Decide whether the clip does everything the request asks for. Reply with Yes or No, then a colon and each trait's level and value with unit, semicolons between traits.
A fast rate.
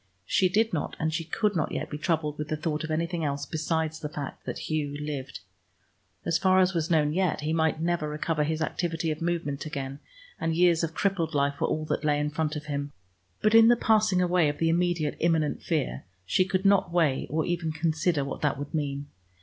Yes: fast, 220 wpm